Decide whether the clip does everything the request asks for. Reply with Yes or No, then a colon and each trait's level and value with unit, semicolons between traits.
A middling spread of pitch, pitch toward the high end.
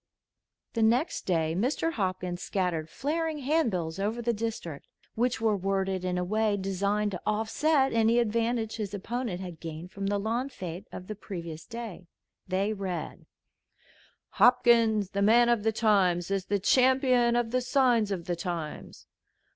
Yes: average, 4.3 semitones; high, 210 Hz